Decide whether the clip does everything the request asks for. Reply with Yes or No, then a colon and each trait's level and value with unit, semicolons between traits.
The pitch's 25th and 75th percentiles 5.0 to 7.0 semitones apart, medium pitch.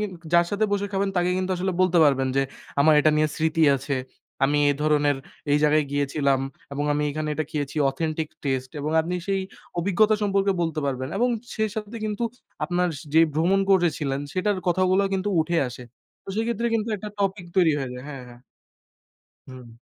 Yes: average, 5.3 semitones; medium, 165 Hz